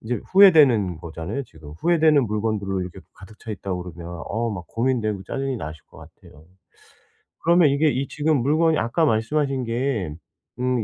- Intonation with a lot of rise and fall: Yes, wide, 6.9 semitones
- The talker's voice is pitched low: Yes, low, 115 Hz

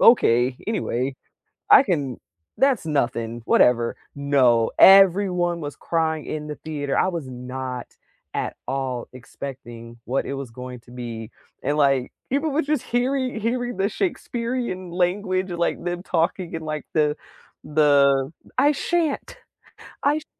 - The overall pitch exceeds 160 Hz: No, medium, 155 Hz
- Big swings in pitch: Yes, wide, 6.8 semitones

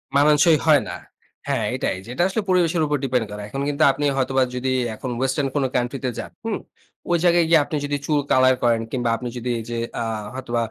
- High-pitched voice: No, low, 135 Hz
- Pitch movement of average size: Yes, average, 3.6 semitones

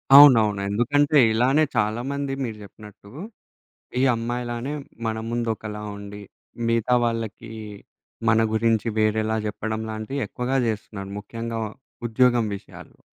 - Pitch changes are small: Yes, narrow, 2.1 semitones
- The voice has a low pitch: Yes, low, 115 Hz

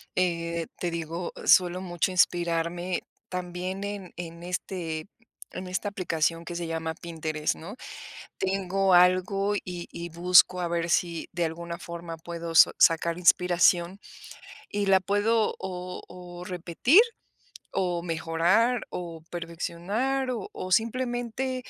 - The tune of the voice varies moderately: No, narrow, 2.1 semitones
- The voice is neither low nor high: Yes, medium, 175 Hz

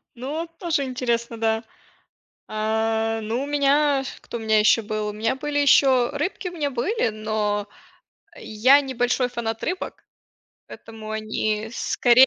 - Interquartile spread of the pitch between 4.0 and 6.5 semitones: Yes, average, 4.3 semitones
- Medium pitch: No, high, 235 Hz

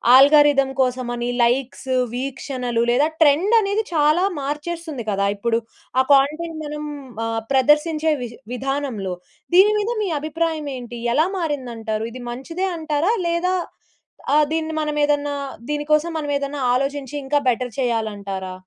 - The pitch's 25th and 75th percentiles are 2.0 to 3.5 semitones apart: No, average, 3.9 semitones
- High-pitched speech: Yes, very high, 285 Hz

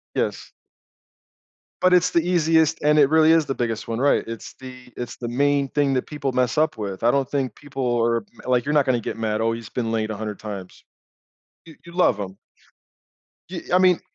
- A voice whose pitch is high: No, low, 130 Hz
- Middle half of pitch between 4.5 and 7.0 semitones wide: Yes, average, 4.9 semitones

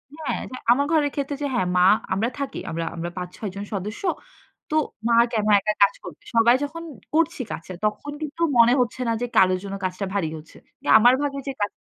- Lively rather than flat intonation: Yes, wide, 6.5 semitones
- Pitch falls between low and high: No, high, 230 Hz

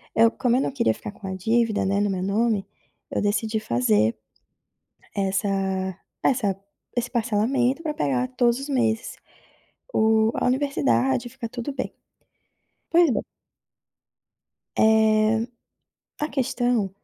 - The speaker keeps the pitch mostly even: No, average, 3.9 semitones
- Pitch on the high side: Yes, high, 220 Hz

